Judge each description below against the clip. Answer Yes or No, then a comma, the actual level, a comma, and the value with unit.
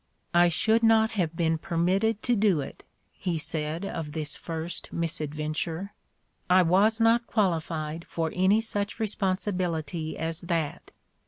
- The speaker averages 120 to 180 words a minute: Yes, average, 145 wpm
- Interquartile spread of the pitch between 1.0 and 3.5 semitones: No, average, 4.1 semitones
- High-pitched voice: No, medium, 175 Hz